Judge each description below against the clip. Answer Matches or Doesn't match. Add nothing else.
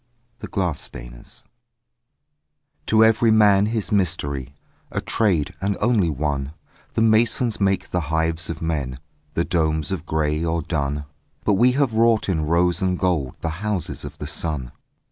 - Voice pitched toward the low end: Matches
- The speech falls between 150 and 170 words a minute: Matches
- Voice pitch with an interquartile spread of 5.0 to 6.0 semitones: Matches